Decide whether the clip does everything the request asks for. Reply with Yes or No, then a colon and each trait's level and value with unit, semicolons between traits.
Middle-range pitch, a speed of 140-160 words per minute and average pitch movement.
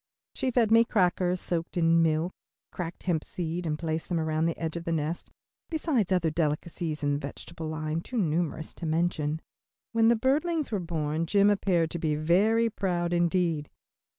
No: medium, 170 Hz; average, 180 wpm; average, 3.4 semitones